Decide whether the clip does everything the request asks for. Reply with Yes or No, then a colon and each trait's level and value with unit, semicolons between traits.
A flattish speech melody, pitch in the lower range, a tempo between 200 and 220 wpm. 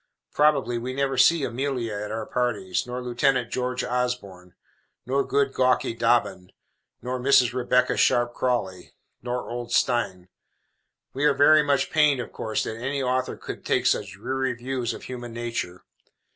No: narrow, 2.2 semitones; low, 125 Hz; average, 155 wpm